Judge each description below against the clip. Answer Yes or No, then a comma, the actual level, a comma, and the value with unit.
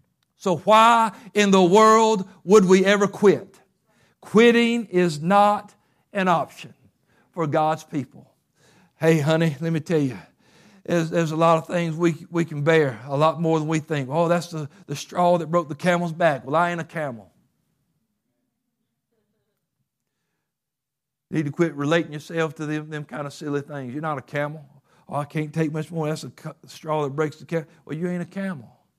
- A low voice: No, medium, 160 Hz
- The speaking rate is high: No, average, 185 wpm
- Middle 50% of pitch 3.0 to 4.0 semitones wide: No, narrow, 2.6 semitones